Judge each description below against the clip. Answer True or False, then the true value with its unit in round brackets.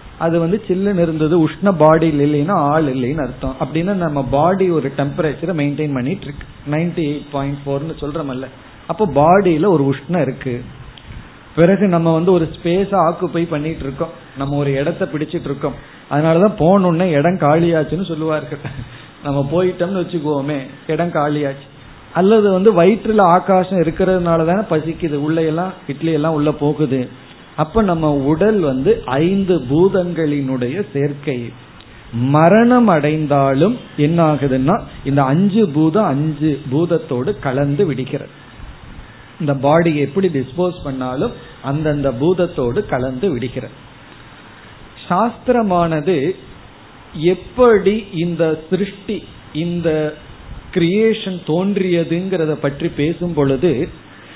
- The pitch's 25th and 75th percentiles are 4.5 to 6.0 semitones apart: False (3.9 semitones)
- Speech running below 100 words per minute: False (105 wpm)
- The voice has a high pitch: False (155 Hz)